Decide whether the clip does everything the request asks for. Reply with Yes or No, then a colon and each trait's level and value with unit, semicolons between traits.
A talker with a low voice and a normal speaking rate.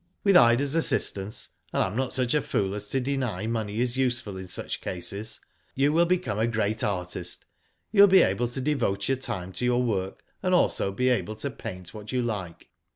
No: low, 115 Hz; fast, 210 wpm